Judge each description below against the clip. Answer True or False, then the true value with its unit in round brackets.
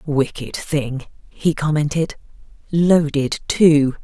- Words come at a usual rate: False (75 wpm)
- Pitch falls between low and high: True (150 Hz)